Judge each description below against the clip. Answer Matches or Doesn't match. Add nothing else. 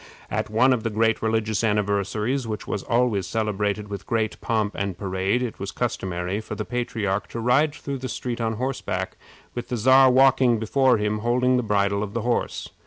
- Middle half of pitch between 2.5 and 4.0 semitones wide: Matches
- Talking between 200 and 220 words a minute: Doesn't match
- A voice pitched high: Doesn't match